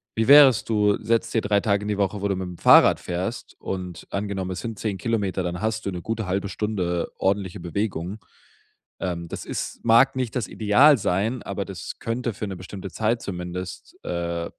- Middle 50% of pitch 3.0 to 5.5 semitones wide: Yes, average, 3.3 semitones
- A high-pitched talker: No, low, 100 Hz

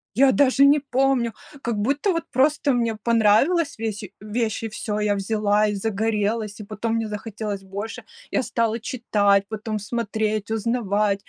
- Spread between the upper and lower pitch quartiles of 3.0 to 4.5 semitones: No, narrow, 2.6 semitones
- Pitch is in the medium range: No, high, 220 Hz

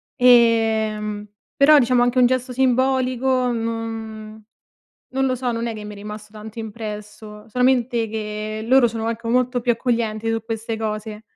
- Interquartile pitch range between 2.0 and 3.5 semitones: Yes, narrow, 2.5 semitones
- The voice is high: Yes, high, 230 Hz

